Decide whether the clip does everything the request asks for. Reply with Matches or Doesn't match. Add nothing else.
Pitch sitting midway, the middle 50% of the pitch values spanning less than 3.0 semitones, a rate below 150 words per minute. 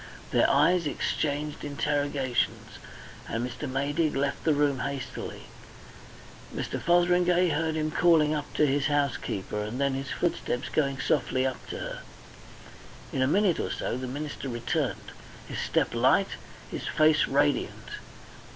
Matches